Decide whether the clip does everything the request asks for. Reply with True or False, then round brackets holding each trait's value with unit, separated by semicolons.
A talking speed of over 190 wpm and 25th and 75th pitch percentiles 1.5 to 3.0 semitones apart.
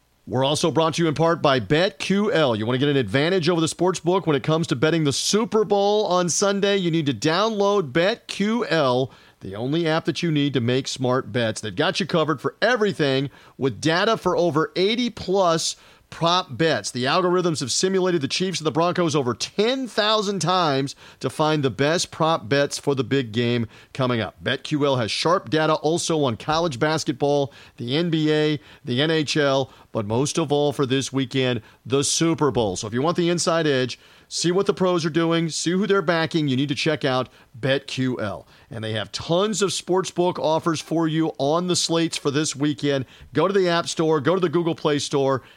False (200 wpm; 4.3 semitones)